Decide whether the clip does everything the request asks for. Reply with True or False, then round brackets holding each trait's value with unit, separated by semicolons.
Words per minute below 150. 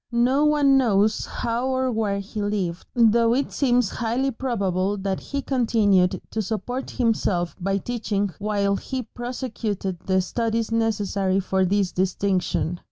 True (140 wpm)